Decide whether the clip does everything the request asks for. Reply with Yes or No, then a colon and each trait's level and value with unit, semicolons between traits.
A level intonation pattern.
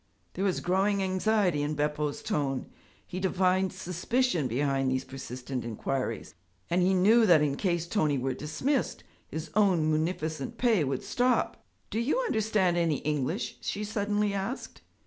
No: wide, 5.6 semitones